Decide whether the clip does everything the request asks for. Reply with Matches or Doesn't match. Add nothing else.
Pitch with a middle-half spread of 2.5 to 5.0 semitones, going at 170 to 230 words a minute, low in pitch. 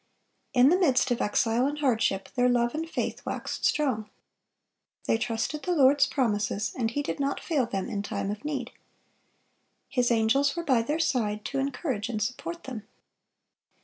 Doesn't match